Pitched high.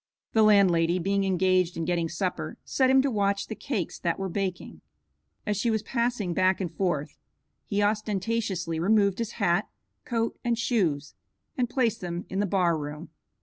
Yes: high, 195 Hz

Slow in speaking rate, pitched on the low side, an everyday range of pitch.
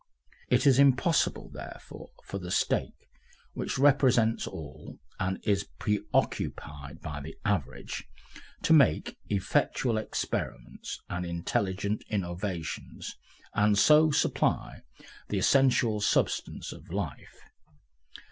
No: slow, 100 wpm; low, 105 Hz; wide, 6.5 semitones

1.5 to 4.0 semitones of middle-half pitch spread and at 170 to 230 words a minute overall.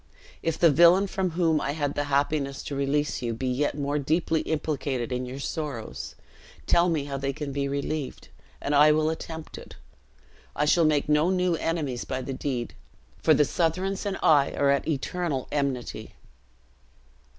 Yes: average, 2.7 semitones; average, 175 wpm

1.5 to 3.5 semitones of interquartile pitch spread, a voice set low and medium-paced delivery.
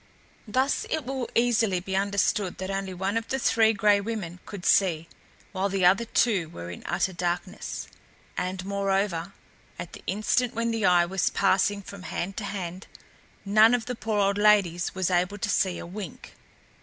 No: average, 2.8 semitones; high, 195 Hz; average, 180 wpm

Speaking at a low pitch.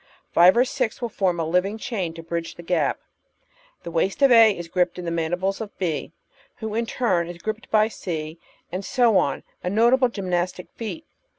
No: medium, 185 Hz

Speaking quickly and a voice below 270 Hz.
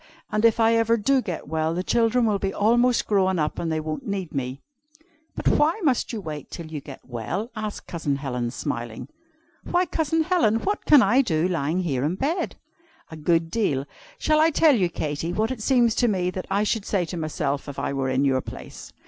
Yes: fast, 215 wpm; medium, 185 Hz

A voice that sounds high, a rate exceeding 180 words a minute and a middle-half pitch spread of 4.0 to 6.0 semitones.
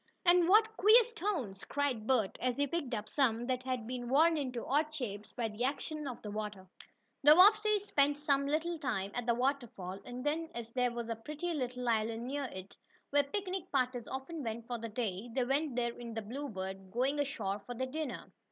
Yes: very high, 255 Hz; fast, 205 wpm; average, 4.4 semitones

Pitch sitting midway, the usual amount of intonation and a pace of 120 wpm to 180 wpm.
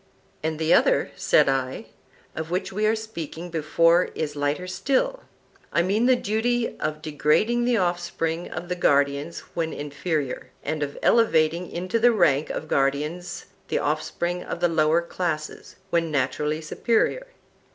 Yes: medium, 165 Hz; average, 3.3 semitones; average, 145 wpm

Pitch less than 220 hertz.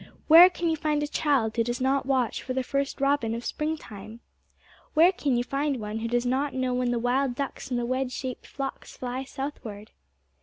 No: very high, 260 Hz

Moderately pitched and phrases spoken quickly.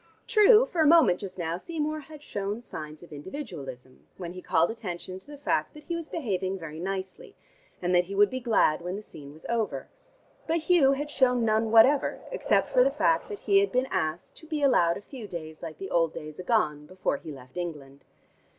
No: high, 200 Hz; fast, 215 wpm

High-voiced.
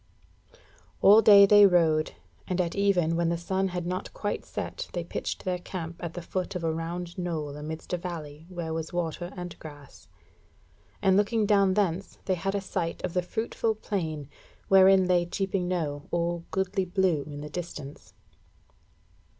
No: medium, 175 Hz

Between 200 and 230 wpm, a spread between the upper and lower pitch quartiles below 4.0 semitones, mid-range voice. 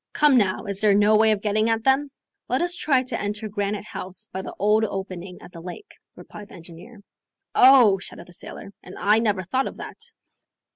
No: fast, 205 wpm; average, 3.0 semitones; high, 210 Hz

